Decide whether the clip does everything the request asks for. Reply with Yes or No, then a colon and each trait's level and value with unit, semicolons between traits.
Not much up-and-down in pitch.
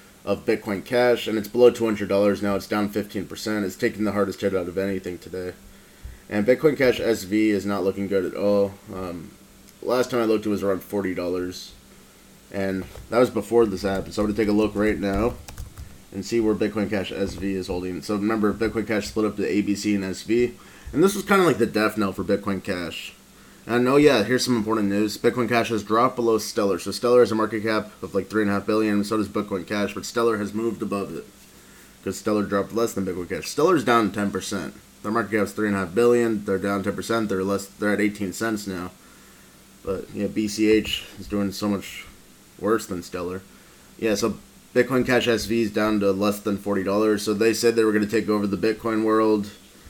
Yes: narrow, 2.2 semitones